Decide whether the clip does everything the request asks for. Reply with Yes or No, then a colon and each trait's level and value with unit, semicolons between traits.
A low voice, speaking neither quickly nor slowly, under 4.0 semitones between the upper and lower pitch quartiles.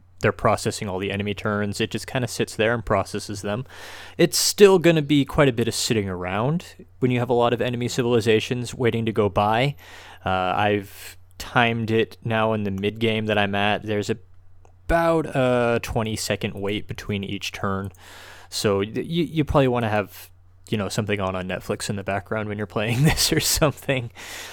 Yes: low, 110 Hz; average, 195 wpm; average, 3.6 semitones